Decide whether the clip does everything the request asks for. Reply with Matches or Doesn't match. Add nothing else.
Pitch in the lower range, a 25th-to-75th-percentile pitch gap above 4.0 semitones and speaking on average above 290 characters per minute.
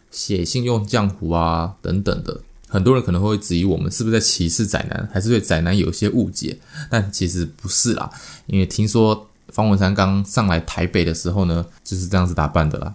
Doesn't match